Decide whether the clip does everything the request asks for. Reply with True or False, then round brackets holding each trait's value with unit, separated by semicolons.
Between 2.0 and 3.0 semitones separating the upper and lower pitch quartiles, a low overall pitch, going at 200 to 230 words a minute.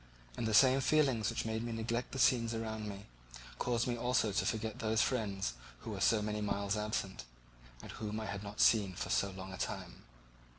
True (2.4 semitones; 110 Hz; 205 wpm)